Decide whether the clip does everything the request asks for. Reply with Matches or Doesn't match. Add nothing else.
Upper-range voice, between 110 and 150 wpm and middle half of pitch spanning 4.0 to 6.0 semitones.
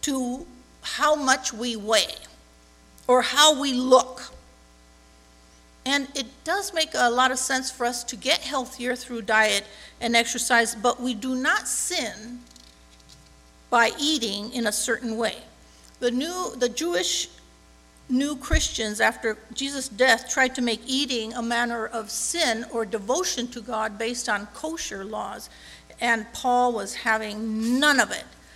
Doesn't match